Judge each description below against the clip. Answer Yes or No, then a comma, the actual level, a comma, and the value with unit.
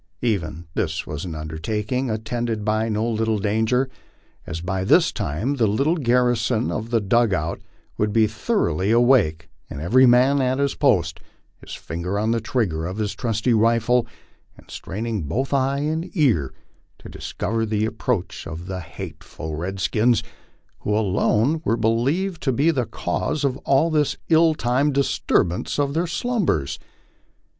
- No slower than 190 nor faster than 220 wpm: No, average, 160 wpm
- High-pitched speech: No, low, 115 Hz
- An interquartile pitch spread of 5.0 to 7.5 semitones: Yes, average, 5.3 semitones